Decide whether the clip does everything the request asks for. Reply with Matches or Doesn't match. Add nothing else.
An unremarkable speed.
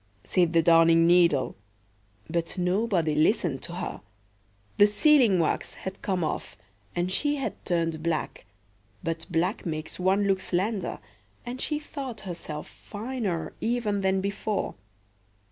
Doesn't match